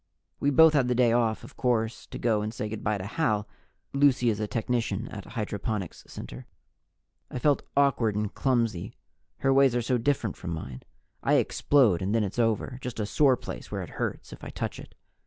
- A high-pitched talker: No, low, 115 Hz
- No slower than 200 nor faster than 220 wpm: Yes, fast, 205 wpm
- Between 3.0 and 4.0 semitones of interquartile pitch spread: Yes, average, 3.3 semitones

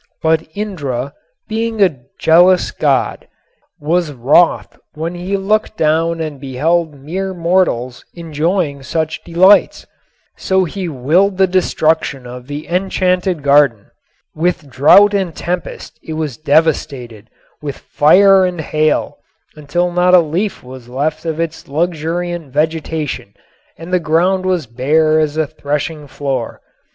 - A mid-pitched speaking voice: Yes, medium, 160 Hz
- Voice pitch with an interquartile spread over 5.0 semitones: No, average, 3.7 semitones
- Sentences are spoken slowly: Yes, slow, 130 wpm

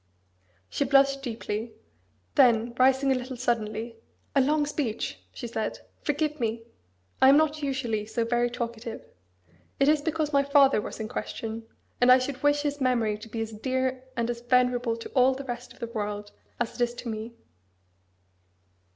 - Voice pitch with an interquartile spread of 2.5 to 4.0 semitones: Yes, average, 3.2 semitones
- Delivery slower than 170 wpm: No, average, 175 wpm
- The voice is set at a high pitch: Yes, high, 245 Hz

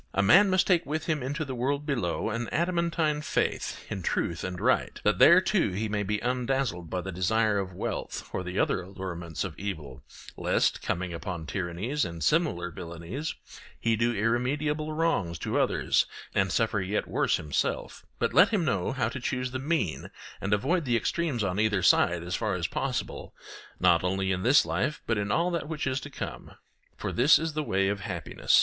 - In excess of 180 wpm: Yes, average, 195 wpm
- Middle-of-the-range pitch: No, low, 110 Hz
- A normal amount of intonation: No, wide, 8.2 semitones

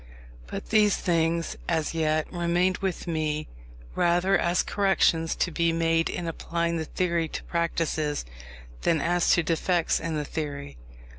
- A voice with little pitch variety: Yes, narrow, 1.5 semitones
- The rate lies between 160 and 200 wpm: No, average, 140 wpm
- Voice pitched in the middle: Yes, medium, 165 Hz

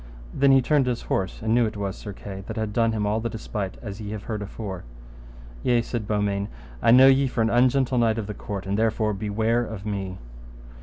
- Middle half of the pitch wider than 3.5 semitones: No, narrow, 2.6 semitones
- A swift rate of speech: Yes, fast, 225 wpm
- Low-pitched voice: Yes, low, 110 Hz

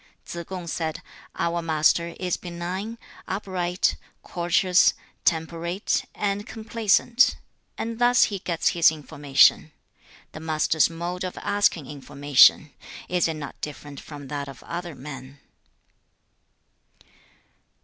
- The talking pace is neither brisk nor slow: No, slow, 115 wpm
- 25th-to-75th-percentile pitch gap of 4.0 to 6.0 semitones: No, average, 3.6 semitones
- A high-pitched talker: No, medium, 170 Hz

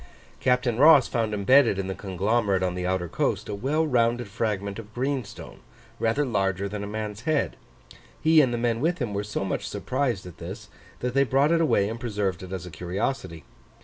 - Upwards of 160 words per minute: Yes, average, 200 wpm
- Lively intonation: No, average, 4.7 semitones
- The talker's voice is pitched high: No, low, 110 Hz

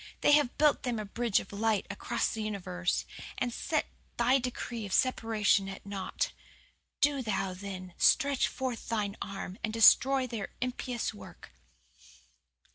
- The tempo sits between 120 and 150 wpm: Yes, average, 145 wpm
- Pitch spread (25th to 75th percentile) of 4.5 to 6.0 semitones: No, average, 4.0 semitones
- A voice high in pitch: Yes, high, 225 Hz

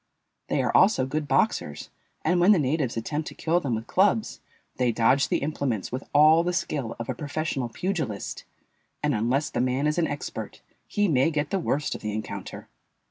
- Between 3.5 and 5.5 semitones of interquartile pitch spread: Yes, average, 4.7 semitones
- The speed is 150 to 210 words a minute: Yes, average, 190 wpm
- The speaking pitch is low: No, medium, 145 Hz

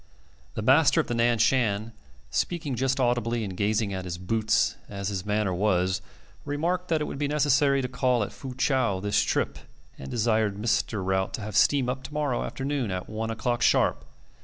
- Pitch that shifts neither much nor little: Yes, average, 4.6 semitones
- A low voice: Yes, low, 115 Hz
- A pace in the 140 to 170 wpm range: No, average, 190 wpm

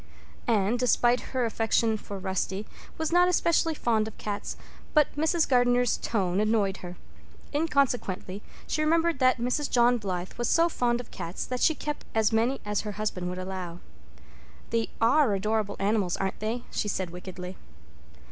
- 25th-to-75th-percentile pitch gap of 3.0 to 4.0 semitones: No, average, 4.6 semitones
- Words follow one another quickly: No, average, 160 wpm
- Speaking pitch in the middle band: No, high, 225 Hz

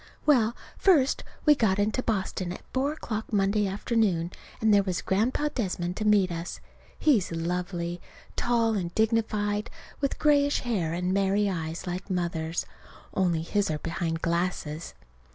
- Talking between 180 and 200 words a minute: No, average, 145 wpm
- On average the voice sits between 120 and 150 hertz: No, high, 195 Hz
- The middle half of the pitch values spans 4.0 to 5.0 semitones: Yes, average, 4.3 semitones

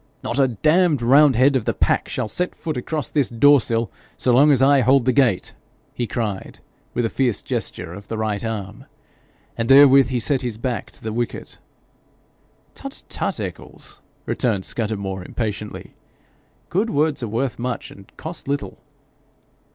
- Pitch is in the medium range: No, low, 125 Hz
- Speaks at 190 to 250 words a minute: No, average, 165 wpm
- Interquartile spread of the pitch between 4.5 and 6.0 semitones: No, average, 3.9 semitones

